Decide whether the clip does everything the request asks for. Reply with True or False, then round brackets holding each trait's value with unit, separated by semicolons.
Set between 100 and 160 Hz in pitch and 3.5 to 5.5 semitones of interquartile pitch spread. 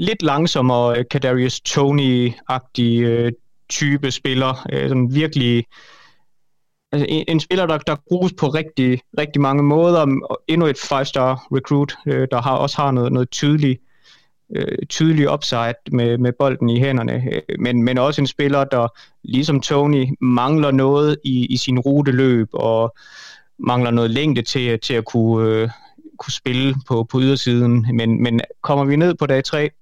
False (135 Hz; 3.1 semitones)